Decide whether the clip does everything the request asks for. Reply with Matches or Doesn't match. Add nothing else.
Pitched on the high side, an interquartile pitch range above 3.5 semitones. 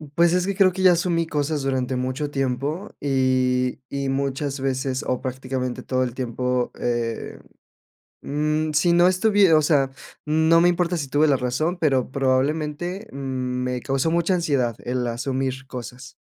Doesn't match